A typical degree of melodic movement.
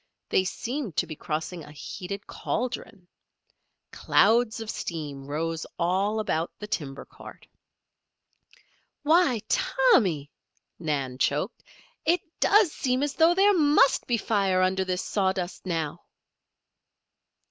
No: wide, 7.2 semitones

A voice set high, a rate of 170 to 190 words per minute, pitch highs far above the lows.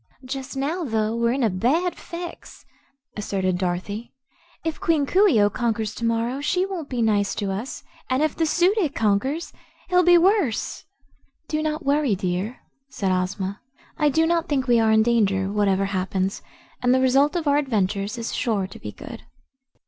Yes: high, 240 Hz; average, 180 wpm; wide, 7.0 semitones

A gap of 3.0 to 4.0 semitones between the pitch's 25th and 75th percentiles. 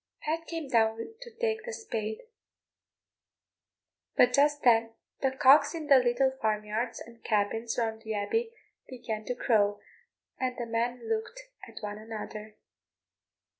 No: average, 4.7 semitones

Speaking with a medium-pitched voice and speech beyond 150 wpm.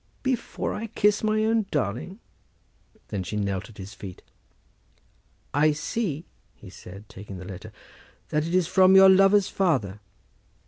No: medium, 155 Hz; average, 140 wpm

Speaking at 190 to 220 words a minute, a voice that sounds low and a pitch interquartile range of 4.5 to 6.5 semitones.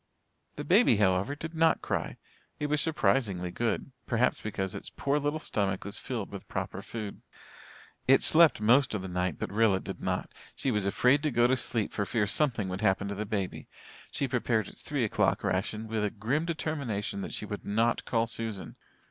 Yes: average, 195 wpm; low, 110 Hz; wide, 5.4 semitones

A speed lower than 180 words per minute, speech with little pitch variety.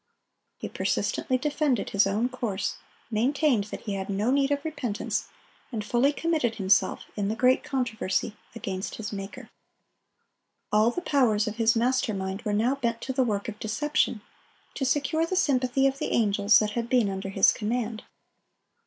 No: average, 170 wpm; average, 4.2 semitones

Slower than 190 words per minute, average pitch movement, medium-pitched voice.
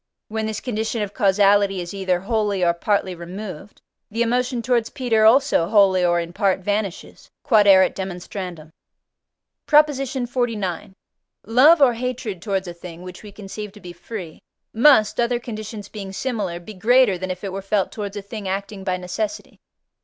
No: average, 160 wpm; average, 3.4 semitones; high, 205 Hz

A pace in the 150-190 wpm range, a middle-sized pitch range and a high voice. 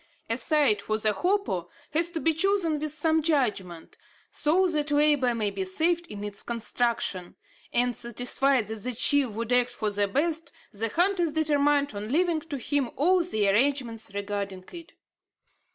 No: average, 165 wpm; wide, 6.7 semitones; very high, 265 Hz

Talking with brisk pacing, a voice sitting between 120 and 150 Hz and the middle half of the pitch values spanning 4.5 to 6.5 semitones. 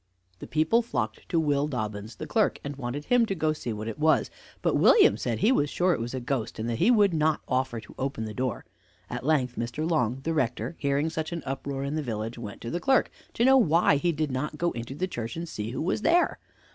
Yes: fast, 250 wpm; medium, 140 Hz; average, 5.3 semitones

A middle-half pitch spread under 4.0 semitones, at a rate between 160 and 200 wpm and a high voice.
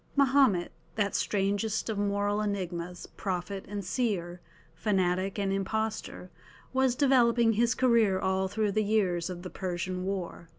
No: average, 3.0 semitones; slow, 135 wpm; high, 200 Hz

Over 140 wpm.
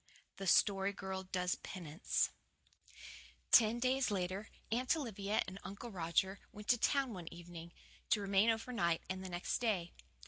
Yes: average, 150 wpm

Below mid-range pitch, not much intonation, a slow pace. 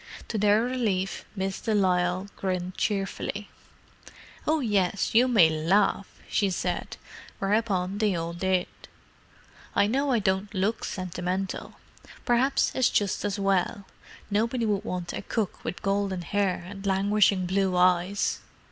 No: high, 195 Hz; narrow, 2.3 semitones; slow, 130 wpm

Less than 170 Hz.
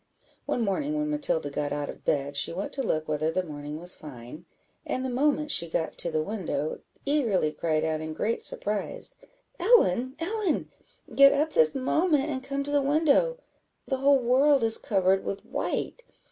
No: high, 230 Hz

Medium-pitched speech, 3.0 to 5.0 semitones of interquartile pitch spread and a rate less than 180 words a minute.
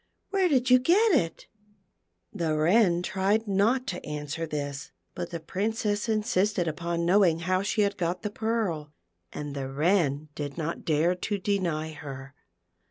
No: medium, 175 Hz; wide, 5.4 semitones; average, 160 wpm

